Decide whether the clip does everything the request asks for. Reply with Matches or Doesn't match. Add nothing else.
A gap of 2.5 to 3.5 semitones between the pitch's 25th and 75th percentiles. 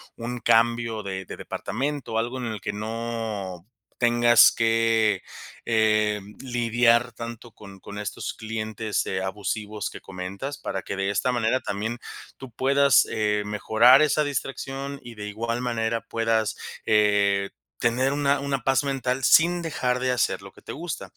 Matches